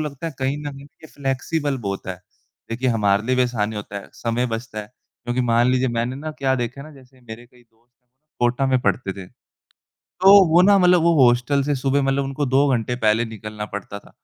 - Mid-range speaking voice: No, low, 125 Hz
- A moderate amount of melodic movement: Yes, average, 3.4 semitones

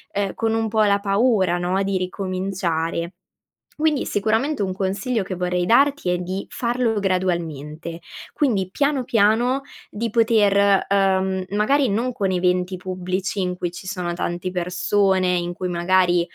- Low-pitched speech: No, high, 190 Hz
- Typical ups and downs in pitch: Yes, average, 3.2 semitones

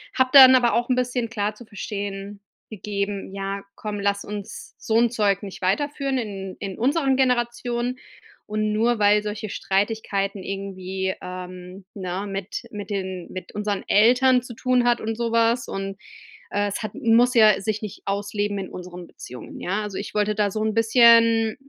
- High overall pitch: Yes, high, 210 Hz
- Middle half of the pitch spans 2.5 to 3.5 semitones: Yes, average, 3.0 semitones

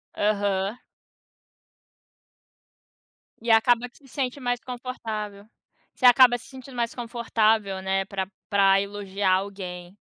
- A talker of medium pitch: No, high, 215 Hz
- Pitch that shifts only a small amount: No, average, 3.8 semitones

